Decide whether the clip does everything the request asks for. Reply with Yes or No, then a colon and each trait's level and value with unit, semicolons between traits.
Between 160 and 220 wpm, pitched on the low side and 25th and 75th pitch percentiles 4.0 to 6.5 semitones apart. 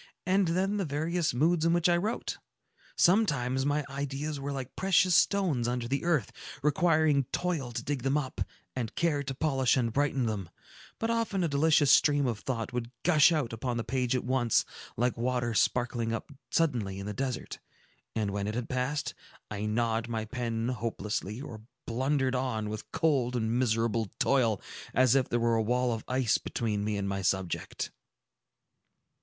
Yes: average, 175 wpm; low, 130 Hz; average, 4.5 semitones